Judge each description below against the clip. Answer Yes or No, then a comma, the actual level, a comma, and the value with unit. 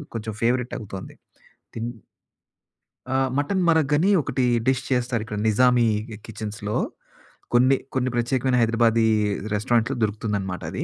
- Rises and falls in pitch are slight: No, average, 3.0 semitones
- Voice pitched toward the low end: Yes, low, 120 Hz